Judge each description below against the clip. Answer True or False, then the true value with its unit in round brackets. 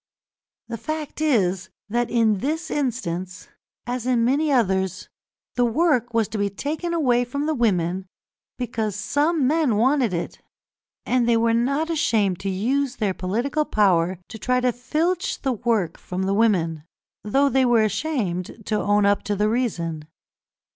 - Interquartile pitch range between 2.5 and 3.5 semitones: False (5.3 semitones)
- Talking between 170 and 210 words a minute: False (160 wpm)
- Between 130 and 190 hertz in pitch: False (230 Hz)